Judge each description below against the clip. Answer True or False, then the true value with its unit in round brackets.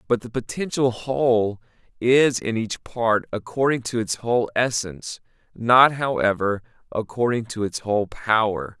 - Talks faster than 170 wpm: False (135 wpm)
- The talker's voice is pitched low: True (115 Hz)